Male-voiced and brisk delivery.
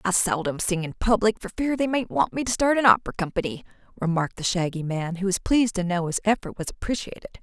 No: female; fast, 235 wpm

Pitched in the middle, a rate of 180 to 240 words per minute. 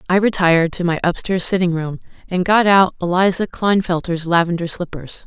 No: medium, 180 Hz; average, 160 wpm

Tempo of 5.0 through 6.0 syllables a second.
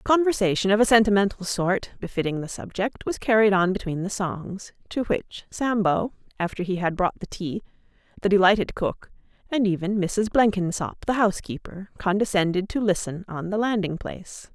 Yes: 5.2 syllables/s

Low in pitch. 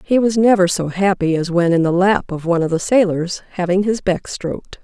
No: medium, 185 Hz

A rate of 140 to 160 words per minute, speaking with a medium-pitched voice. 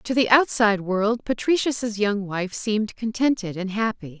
No: average, 155 wpm; high, 215 Hz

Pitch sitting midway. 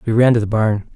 No: low, 110 Hz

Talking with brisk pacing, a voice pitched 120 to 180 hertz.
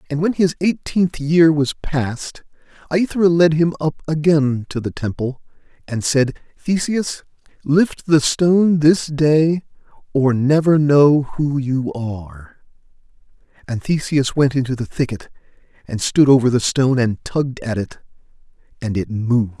No: average, 145 wpm; medium, 140 Hz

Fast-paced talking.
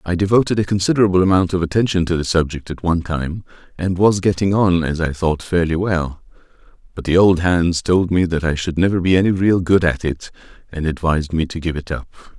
Yes: fast, 220 wpm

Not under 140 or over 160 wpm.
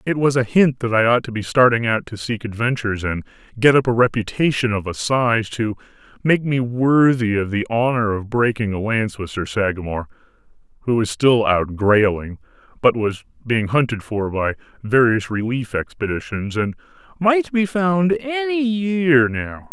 No: average, 175 wpm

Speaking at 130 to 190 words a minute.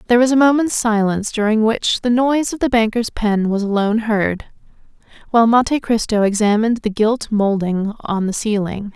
Yes: average, 175 wpm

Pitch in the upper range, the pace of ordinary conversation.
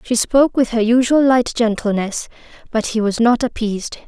Yes: high, 230 Hz; average, 175 wpm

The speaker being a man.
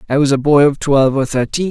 Yes: male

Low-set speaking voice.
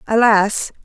No: high, 215 Hz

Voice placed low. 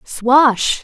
No: very high, 250 Hz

